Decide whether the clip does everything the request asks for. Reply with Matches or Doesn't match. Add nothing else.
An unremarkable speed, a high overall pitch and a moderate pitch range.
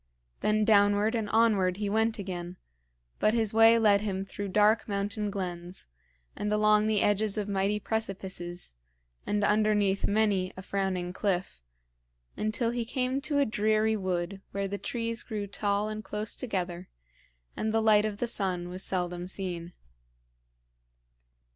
Doesn't match